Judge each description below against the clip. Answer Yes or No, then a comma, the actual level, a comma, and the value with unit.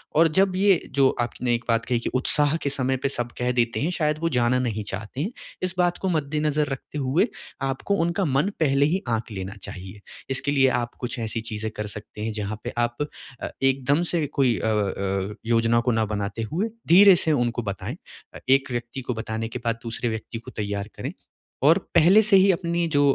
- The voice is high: No, low, 125 Hz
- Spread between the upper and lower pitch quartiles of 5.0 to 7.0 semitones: Yes, average, 5.3 semitones